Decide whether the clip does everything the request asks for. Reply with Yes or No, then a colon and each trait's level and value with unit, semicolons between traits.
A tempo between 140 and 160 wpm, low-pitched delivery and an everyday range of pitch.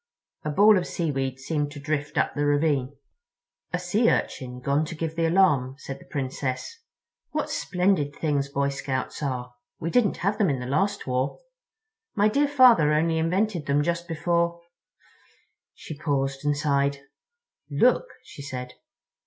No: average, 155 wpm; medium, 150 Hz; average, 3.8 semitones